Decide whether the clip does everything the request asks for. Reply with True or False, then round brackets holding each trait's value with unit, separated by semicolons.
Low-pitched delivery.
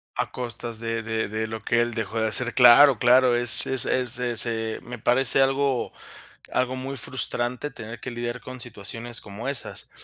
True (120 Hz)